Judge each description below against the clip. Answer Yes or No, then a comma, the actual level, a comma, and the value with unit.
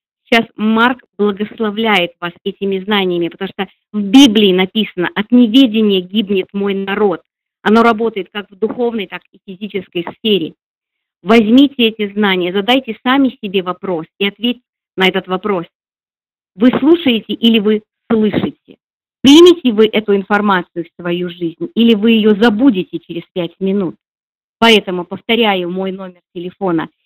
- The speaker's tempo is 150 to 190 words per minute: No, average, 140 wpm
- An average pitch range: Yes, average, 3.5 semitones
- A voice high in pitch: Yes, high, 205 Hz